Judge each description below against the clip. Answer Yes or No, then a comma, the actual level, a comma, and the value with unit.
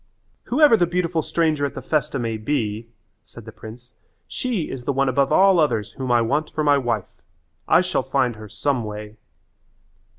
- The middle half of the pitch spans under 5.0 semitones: No, wide, 5.5 semitones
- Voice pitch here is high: No, low, 135 Hz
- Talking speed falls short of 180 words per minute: No, average, 185 wpm